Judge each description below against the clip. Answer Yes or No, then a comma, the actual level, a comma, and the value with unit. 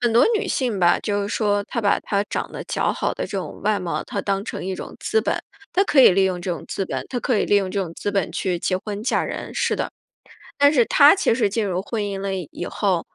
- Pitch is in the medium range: No, high, 200 Hz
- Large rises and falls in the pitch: No, average, 3.4 semitones